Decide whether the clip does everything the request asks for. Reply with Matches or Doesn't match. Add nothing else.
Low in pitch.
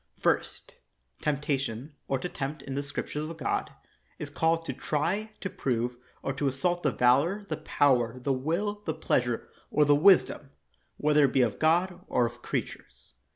Doesn't match